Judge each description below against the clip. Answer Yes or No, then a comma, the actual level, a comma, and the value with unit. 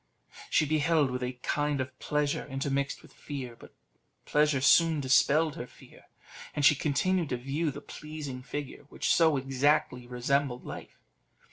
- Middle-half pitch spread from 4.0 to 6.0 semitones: No, narrow, 2.5 semitones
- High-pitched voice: No, medium, 140 Hz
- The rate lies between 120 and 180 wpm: Yes, average, 150 wpm